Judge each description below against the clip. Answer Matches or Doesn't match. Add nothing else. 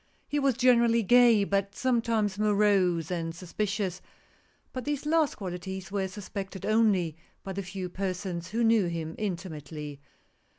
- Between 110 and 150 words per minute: Matches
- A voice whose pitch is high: Matches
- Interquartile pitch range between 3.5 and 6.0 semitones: Matches